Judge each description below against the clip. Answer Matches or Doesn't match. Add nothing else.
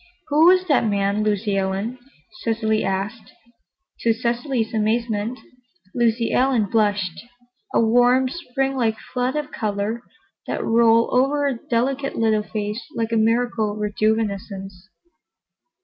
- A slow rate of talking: Matches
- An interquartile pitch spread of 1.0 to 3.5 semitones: Matches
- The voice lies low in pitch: Doesn't match